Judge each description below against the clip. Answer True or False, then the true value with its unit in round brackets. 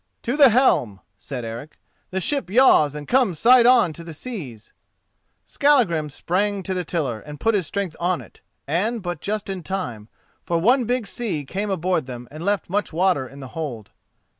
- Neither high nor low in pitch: True (180 Hz)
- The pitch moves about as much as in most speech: False (6.2 semitones)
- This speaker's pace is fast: False (190 wpm)